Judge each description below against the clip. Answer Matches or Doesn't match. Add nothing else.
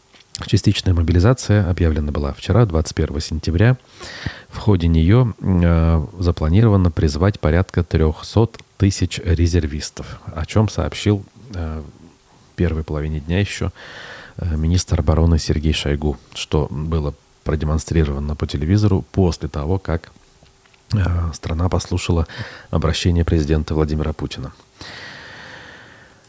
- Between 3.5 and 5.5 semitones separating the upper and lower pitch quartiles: Matches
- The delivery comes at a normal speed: Doesn't match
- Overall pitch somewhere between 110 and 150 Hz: Doesn't match